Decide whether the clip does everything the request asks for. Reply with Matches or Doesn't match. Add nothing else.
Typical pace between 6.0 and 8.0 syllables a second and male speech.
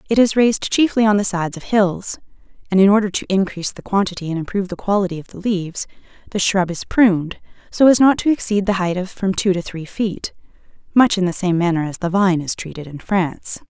Doesn't match